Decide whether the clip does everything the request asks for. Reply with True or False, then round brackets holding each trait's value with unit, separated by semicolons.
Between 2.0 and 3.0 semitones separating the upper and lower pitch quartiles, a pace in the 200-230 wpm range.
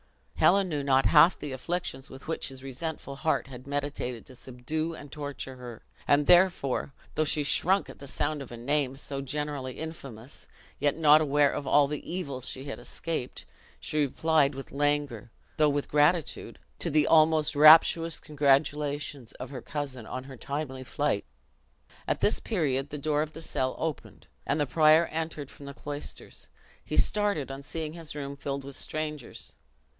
False (2.4 semitones; 170 wpm)